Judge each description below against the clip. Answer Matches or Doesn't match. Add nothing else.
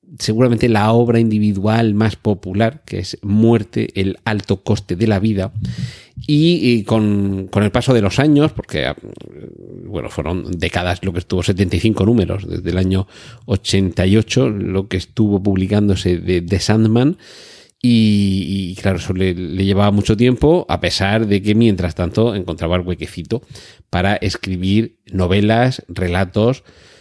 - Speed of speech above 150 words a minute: Doesn't match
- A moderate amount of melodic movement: Matches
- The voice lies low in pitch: Matches